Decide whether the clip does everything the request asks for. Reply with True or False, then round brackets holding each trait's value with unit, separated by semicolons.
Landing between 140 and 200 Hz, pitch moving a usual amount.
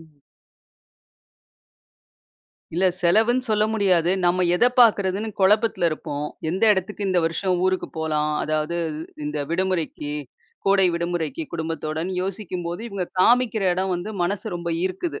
True (185 Hz; 3.1 semitones)